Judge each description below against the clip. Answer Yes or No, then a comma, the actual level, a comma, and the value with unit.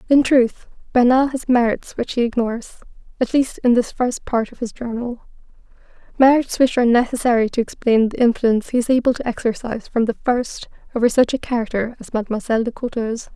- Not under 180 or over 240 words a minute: Yes, average, 185 wpm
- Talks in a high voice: Yes, high, 240 Hz